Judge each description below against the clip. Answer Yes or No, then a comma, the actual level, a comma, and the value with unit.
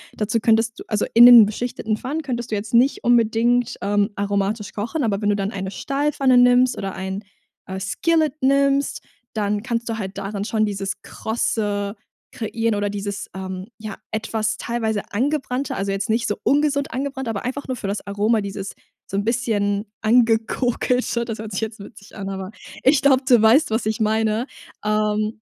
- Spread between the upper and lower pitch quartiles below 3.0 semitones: No, average, 3.3 semitones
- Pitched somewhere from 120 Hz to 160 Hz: No, high, 220 Hz